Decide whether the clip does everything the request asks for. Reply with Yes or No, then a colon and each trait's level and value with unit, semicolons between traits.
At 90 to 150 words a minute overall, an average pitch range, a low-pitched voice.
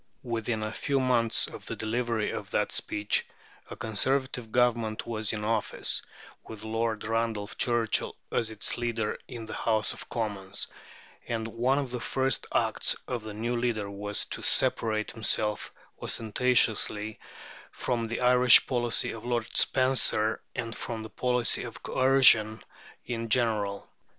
No: average, 145 wpm; narrow, 2.0 semitones; low, 115 Hz